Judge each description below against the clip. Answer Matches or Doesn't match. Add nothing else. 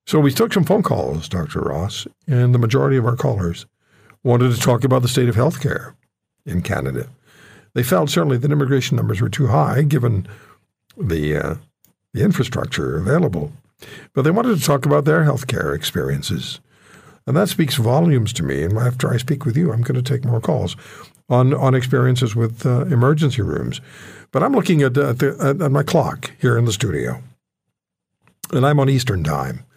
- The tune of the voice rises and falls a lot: Doesn't match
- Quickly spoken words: Doesn't match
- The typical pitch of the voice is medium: Doesn't match